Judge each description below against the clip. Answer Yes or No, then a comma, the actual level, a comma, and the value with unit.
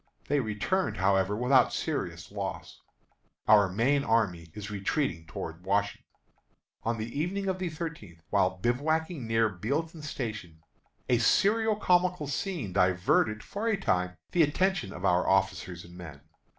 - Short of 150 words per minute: Yes, average, 140 wpm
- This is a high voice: No, low, 115 Hz